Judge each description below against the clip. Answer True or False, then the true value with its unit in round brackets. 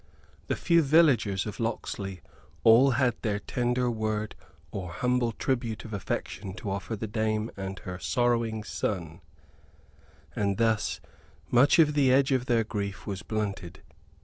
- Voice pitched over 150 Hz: False (110 Hz)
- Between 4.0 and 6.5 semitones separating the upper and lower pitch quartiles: False (3.6 semitones)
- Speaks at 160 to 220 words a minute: False (145 wpm)